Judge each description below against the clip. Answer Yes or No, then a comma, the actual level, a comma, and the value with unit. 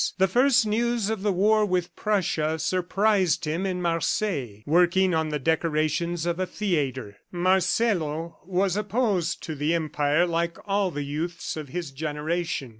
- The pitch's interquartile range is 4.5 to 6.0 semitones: No, average, 3.8 semitones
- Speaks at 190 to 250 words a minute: No, average, 150 wpm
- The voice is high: No, medium, 175 Hz